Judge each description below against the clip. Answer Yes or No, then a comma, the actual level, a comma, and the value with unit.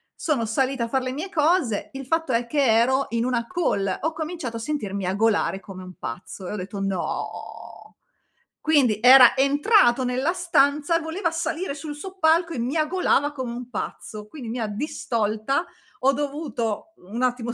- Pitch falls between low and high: No, very high, 260 Hz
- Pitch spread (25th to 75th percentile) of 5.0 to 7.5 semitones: Yes, average, 5.3 semitones